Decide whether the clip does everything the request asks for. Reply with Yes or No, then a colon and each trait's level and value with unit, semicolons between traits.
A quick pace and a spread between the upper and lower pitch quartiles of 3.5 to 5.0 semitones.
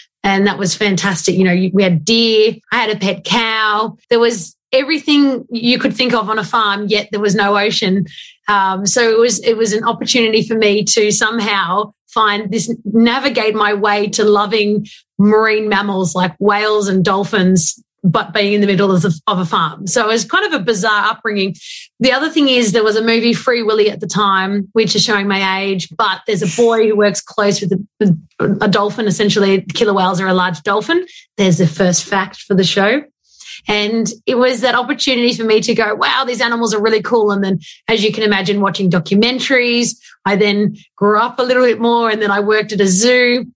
No: fast, 210 wpm; average, 2.7 semitones